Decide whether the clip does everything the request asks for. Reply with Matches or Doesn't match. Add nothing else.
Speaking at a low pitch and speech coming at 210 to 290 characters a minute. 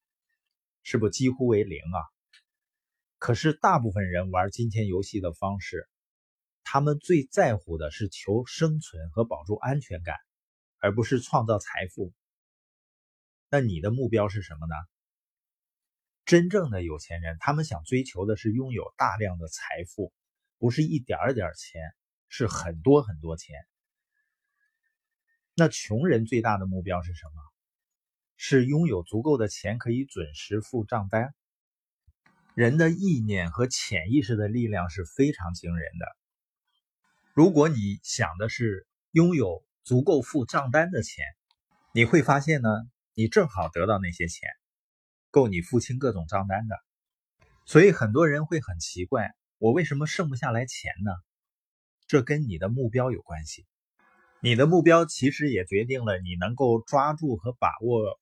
Matches